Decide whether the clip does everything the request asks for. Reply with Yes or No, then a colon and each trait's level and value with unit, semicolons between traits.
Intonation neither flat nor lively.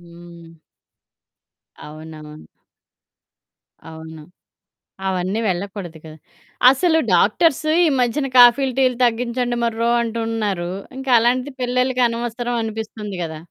No: wide, 6.1 semitones